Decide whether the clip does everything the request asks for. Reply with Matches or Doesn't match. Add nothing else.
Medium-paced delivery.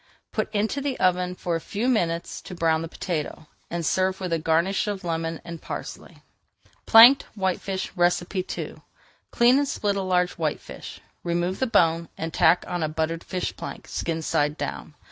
Matches